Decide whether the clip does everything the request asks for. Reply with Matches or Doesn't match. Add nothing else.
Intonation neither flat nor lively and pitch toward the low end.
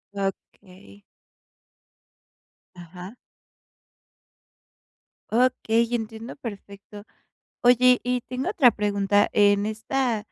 Doesn't match